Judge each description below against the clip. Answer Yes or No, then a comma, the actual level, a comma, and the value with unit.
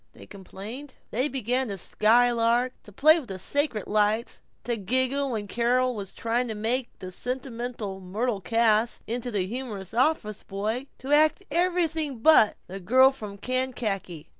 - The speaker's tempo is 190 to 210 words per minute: No, average, 155 wpm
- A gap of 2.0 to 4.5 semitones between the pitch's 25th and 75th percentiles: Yes, average, 3.7 semitones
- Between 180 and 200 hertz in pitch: No, high, 235 Hz